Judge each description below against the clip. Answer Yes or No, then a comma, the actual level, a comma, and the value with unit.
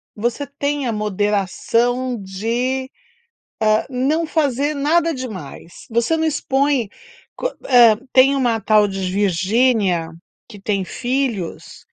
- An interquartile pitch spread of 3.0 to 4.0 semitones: No, average, 4.8 semitones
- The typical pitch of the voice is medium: No, high, 240 Hz